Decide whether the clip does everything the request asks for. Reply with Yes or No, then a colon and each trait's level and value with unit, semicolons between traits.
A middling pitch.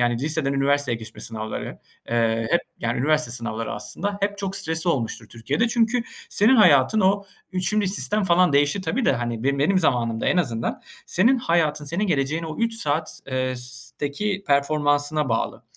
Yes: medium, 150 Hz